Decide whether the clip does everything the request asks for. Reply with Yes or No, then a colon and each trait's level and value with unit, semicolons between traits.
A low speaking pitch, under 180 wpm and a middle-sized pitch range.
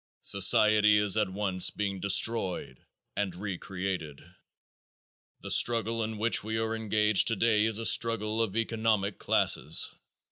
No: low, 105 Hz; slow, 135 wpm; narrow, 2.3 semitones